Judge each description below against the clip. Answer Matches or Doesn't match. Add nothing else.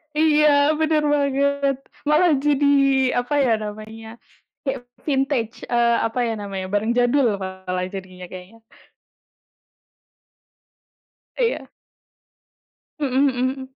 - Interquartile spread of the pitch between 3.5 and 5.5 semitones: Matches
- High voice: Matches